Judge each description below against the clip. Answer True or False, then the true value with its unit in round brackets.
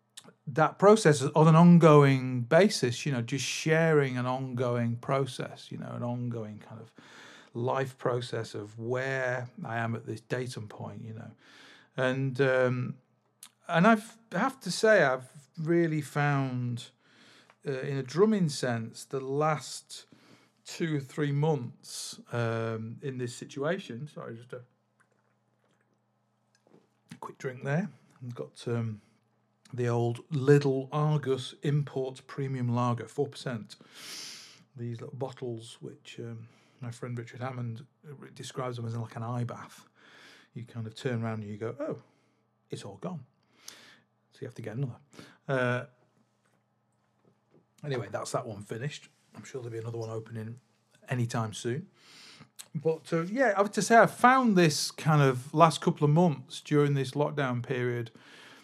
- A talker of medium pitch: False (130 Hz)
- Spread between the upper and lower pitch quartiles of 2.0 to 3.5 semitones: False (4.0 semitones)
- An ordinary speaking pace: True (145 wpm)